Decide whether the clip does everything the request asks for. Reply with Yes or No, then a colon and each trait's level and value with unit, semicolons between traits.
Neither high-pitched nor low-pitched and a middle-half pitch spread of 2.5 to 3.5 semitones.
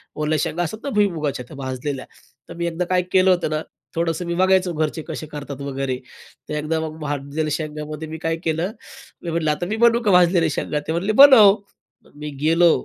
Yes: medium, 160 Hz; average, 3.0 semitones